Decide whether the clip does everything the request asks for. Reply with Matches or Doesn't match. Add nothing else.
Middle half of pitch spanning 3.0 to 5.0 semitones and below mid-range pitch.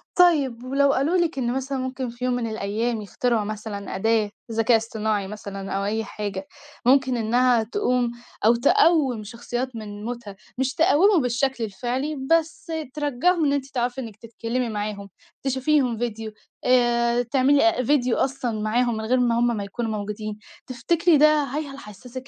Doesn't match